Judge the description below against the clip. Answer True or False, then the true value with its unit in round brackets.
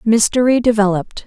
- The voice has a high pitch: True (220 Hz)